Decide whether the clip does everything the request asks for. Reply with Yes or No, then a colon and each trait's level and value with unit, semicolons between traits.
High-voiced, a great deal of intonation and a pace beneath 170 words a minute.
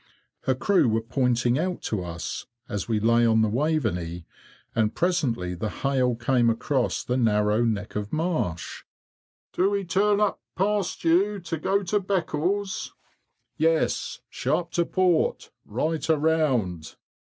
No: low, 135 Hz; wide, 7.8 semitones; average, 140 wpm